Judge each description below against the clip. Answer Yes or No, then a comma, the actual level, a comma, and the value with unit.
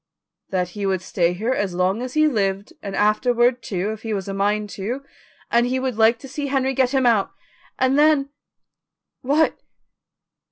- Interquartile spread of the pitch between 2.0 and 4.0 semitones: No, average, 4.8 semitones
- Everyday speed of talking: Yes, average, 190 wpm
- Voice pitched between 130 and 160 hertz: No, high, 225 Hz